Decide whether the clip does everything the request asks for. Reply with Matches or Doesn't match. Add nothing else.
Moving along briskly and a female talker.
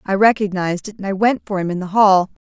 Matches